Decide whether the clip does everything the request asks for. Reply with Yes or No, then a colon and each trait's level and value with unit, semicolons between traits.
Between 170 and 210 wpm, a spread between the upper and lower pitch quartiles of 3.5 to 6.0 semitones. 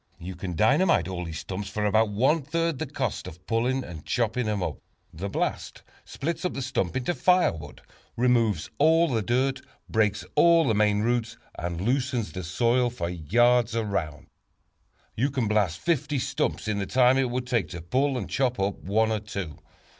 Yes: average, 185 wpm; average, 5.0 semitones